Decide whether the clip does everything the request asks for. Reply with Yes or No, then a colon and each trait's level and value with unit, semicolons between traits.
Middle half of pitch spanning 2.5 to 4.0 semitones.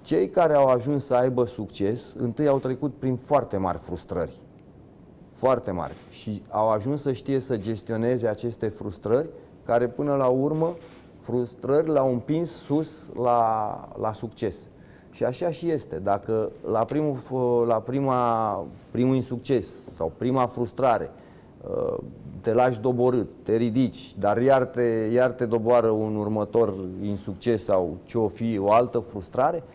Yes: average, 3.2 semitones